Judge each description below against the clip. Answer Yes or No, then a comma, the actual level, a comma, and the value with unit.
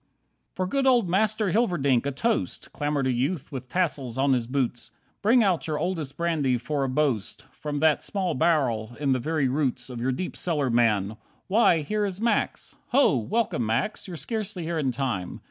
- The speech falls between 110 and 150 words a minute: No, average, 190 wpm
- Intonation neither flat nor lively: No, wide, 6.3 semitones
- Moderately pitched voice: Yes, medium, 150 Hz